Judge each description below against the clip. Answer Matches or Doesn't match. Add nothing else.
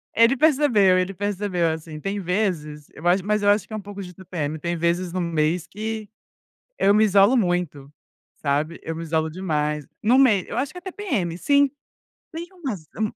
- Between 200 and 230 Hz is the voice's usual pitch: Doesn't match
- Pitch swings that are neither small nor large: Matches